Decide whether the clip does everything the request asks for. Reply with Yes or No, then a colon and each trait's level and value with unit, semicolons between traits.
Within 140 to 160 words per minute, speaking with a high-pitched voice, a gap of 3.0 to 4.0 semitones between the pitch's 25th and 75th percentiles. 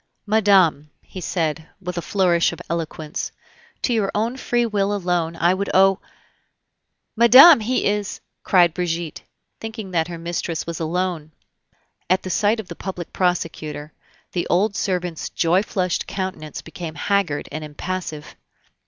No: average, 150 wpm; medium, 180 Hz; average, 3.3 semitones